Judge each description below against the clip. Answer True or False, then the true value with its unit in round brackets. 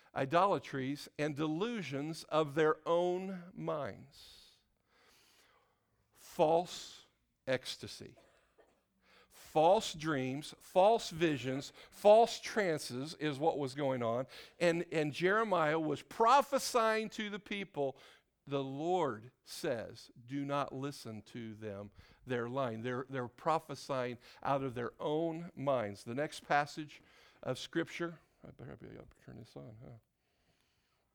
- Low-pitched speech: False (150 Hz)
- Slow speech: True (115 wpm)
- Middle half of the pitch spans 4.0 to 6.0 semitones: True (4.6 semitones)